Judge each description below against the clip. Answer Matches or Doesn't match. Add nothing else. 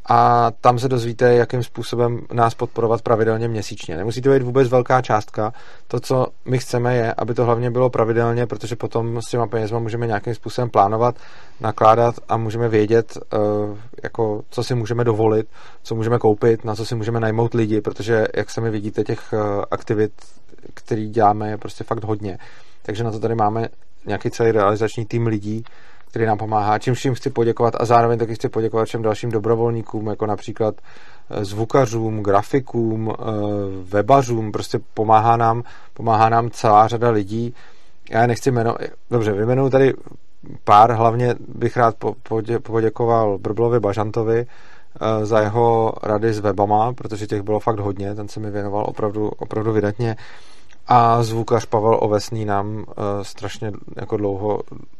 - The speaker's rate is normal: Matches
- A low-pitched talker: Matches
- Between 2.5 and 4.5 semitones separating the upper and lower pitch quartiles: Doesn't match